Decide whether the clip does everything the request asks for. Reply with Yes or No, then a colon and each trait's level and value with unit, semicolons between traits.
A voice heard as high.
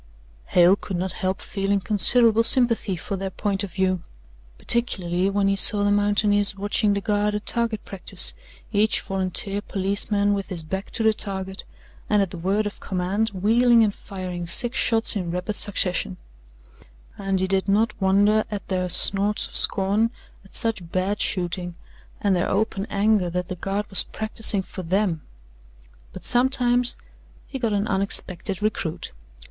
Yes: high, 200 Hz